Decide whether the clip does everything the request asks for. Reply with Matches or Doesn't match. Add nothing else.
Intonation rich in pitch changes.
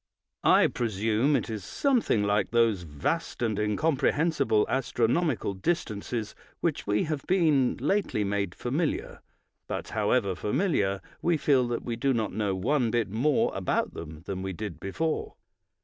Matches